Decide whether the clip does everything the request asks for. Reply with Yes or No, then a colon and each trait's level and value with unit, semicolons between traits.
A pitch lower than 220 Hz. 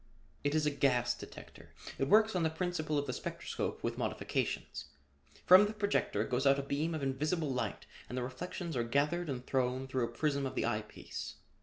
Yes: medium, 140 Hz